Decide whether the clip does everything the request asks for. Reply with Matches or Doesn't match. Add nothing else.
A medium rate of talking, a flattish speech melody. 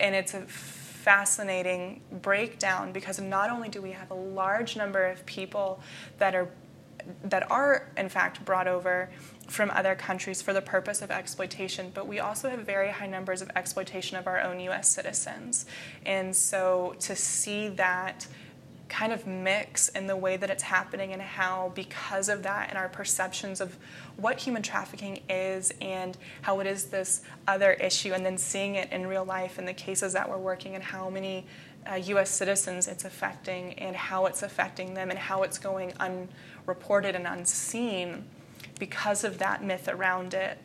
Matches